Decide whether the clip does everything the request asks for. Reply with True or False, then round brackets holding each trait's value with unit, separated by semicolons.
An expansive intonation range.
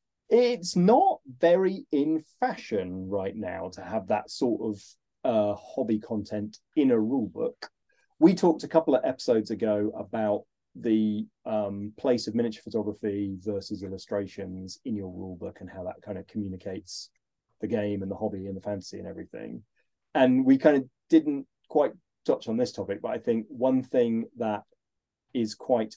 True (7.9 semitones)